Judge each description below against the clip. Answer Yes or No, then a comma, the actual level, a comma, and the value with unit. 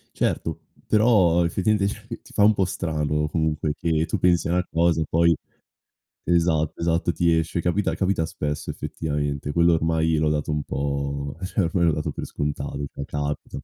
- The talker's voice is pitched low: Yes, very low, 80 Hz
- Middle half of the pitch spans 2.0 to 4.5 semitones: Yes, narrow, 2.6 semitones